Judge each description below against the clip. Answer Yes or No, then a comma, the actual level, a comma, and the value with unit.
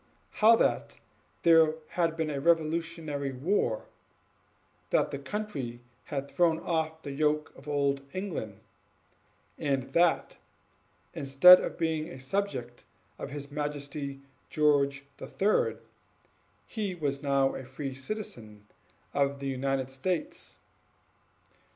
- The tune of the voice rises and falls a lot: No, average, 3.3 semitones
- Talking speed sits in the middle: No, slow, 115 wpm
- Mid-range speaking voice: Yes, medium, 145 Hz